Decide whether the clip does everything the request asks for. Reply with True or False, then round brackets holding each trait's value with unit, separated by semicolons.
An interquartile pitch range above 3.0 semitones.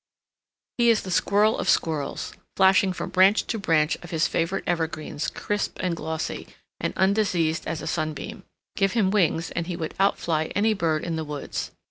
True (3.6 semitones)